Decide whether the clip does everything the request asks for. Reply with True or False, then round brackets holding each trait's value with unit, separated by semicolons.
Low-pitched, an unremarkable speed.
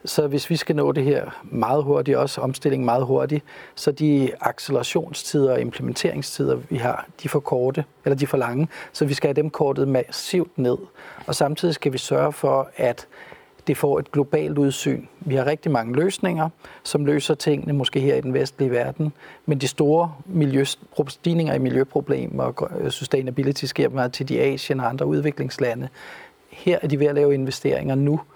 False (145 Hz; 185 wpm)